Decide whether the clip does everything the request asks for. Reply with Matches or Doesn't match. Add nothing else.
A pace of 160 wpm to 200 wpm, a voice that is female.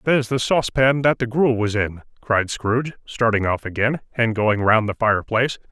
Doesn't match